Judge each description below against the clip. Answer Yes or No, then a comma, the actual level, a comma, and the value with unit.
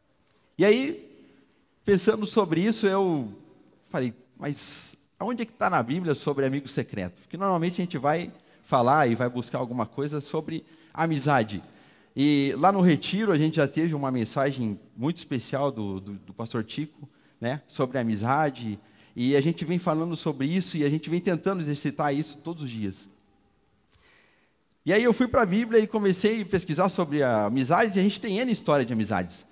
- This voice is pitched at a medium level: Yes, medium, 145 Hz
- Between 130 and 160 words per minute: No, average, 180 wpm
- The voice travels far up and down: Yes, wide, 6.6 semitones